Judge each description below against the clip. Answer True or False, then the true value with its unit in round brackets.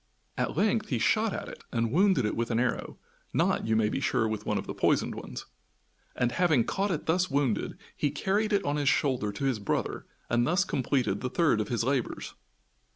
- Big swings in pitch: True (7.3 semitones)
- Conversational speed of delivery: False (215 wpm)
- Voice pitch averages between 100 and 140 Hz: True (135 Hz)